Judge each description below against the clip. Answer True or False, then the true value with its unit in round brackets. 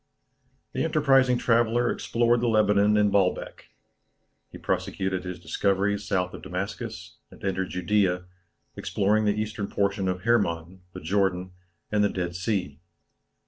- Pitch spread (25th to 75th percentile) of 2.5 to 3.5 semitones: True (2.9 semitones)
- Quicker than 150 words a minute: False (135 wpm)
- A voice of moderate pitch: False (100 Hz)